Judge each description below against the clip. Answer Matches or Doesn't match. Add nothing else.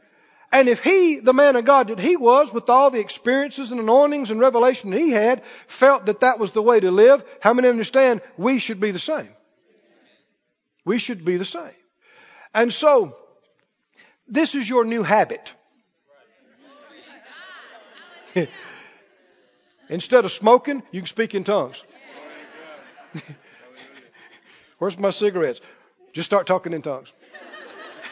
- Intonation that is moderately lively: Doesn't match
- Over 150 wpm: Doesn't match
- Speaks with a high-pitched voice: Matches